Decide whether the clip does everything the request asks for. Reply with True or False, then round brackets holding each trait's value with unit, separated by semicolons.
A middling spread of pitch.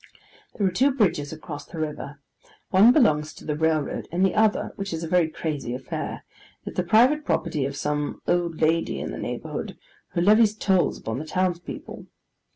True (4.6 semitones)